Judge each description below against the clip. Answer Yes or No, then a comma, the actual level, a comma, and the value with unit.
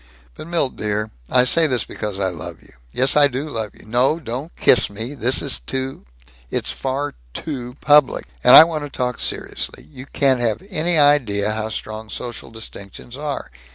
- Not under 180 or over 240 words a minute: Yes, average, 190 wpm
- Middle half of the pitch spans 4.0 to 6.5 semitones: Yes, average, 4.8 semitones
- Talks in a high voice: No, low, 125 Hz